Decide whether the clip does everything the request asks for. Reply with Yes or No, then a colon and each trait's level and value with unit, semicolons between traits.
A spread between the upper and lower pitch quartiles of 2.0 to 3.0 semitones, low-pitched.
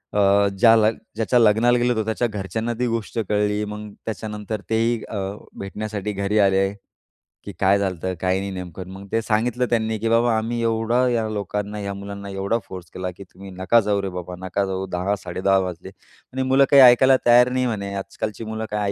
Yes: average, 2.7 semitones; low, 105 Hz